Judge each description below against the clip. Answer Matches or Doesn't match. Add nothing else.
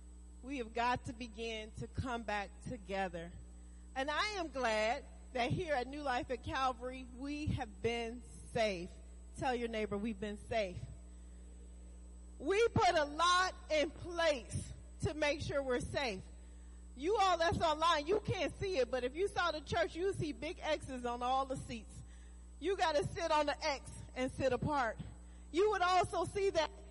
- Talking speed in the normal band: Matches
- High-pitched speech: Matches